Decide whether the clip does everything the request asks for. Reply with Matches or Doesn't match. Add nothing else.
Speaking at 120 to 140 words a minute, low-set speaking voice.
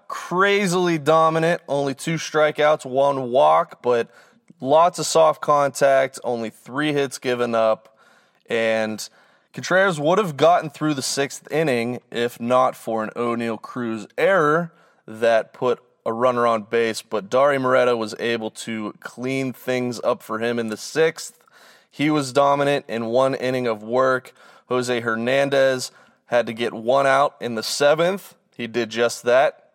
Doesn't match